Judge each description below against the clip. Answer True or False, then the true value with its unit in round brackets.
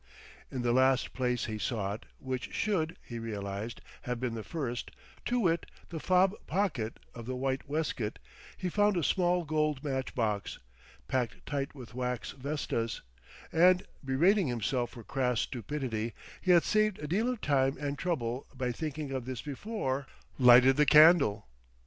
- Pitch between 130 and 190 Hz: True (135 Hz)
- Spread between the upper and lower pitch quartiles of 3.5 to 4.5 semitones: False (5.0 semitones)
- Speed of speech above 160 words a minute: False (155 wpm)